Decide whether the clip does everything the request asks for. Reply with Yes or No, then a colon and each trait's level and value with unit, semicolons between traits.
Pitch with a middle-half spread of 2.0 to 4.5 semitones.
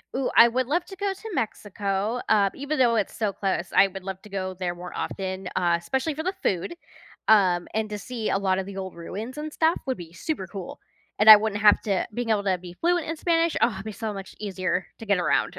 No: average, 5.1 semitones